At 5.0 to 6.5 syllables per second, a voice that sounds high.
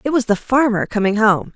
Yes: 5.5 syllables/s; high, 230 Hz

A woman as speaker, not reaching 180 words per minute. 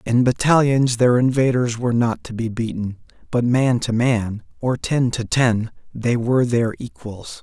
No: male; average, 170 wpm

